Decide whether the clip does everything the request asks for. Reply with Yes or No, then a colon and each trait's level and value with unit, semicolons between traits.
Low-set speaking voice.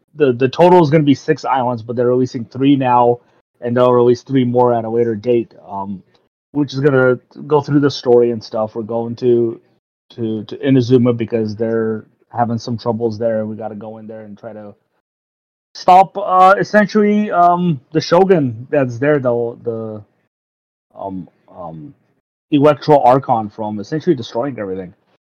Yes: low, 120 Hz